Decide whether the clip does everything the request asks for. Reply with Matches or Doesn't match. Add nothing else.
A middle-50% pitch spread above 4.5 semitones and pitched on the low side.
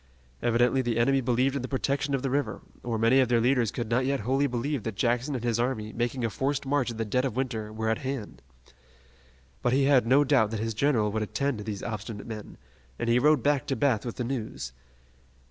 Doesn't match